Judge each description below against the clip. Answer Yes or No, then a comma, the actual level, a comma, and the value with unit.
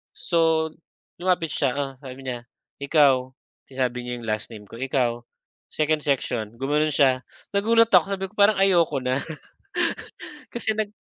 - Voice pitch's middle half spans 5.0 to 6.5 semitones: Yes, average, 5.3 semitones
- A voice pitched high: No, medium, 140 Hz